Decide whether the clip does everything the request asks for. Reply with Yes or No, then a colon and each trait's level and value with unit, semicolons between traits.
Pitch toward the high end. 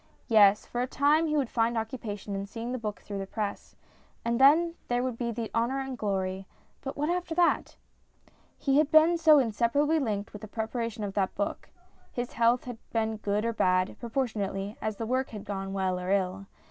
Yes: high, 230 Hz